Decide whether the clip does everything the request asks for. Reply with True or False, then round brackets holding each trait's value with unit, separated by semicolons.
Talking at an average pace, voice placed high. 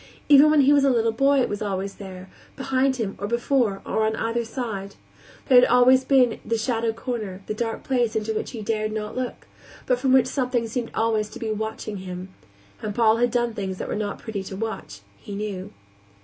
False (215 wpm; 225 Hz)